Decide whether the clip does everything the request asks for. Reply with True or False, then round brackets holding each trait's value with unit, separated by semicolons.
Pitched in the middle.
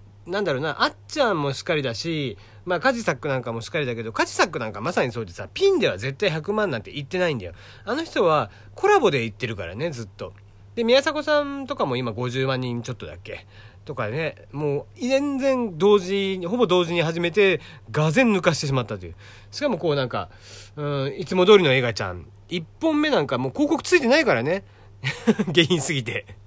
True (145 Hz)